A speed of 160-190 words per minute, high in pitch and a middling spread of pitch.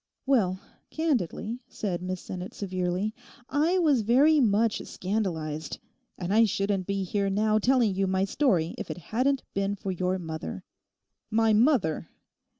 No: average, 145 wpm; high, 200 Hz; average, 4.2 semitones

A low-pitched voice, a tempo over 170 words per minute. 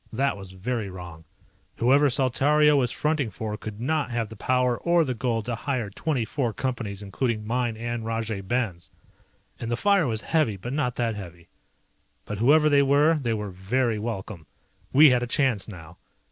Yes: low, 120 Hz; average, 180 wpm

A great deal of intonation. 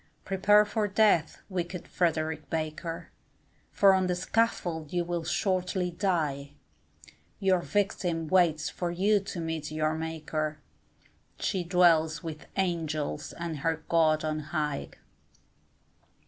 No: average, 2.9 semitones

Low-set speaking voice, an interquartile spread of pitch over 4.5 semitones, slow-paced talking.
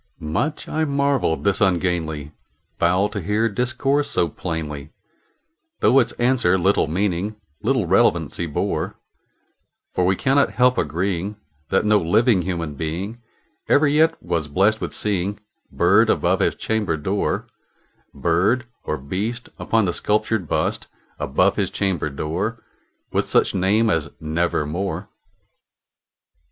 Yes: very low, 95 Hz; average, 5.2 semitones; slow, 125 wpm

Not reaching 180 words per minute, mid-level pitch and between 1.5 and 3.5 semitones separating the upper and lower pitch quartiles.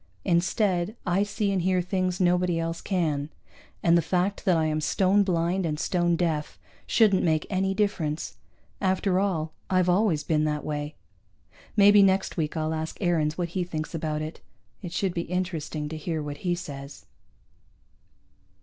Yes: average, 165 wpm; medium, 175 Hz; average, 3.2 semitones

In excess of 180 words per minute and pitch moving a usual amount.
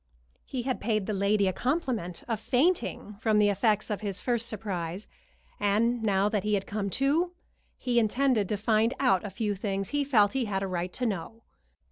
Yes: average, 195 wpm; average, 3.4 semitones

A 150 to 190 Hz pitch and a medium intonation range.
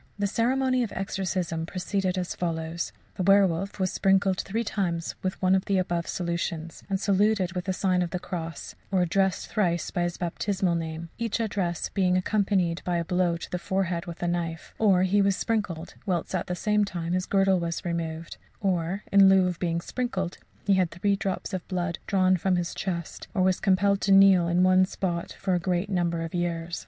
No: medium, 185 Hz; narrow, 2.2 semitones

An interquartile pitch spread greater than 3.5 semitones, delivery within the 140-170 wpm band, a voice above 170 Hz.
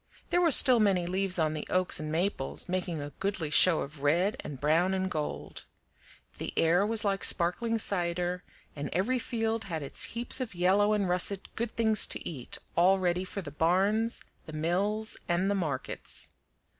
No: average, 3.9 semitones; average, 180 wpm; medium, 185 Hz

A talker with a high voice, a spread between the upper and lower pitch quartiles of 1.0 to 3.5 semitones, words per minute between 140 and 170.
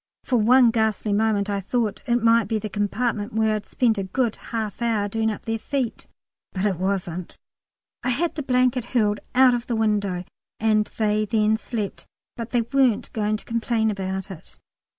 No: high, 220 Hz; narrow, 2.5 semitones; average, 185 wpm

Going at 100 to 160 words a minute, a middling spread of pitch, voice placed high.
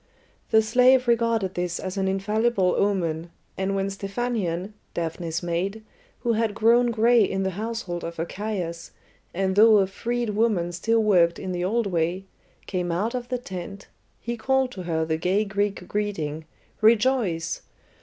Yes: average, 155 wpm; average, 4.3 semitones; high, 195 Hz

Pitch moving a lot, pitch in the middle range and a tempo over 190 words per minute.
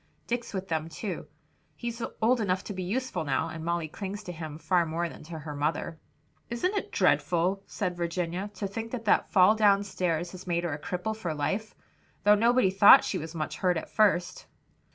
No: average, 4.0 semitones; medium, 180 Hz; average, 200 wpm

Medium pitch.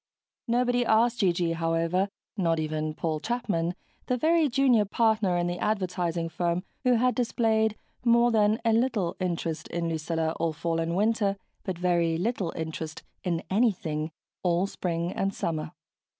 Yes: medium, 180 Hz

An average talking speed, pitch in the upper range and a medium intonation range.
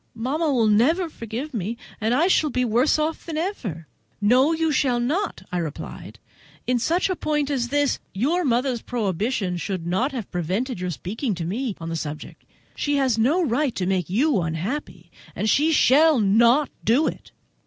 No: average, 185 wpm; high, 245 Hz; wide, 6.6 semitones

